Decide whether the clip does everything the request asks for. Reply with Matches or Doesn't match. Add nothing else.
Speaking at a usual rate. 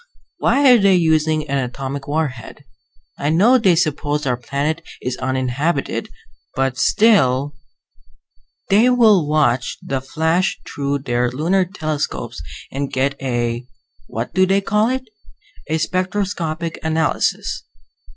Doesn't match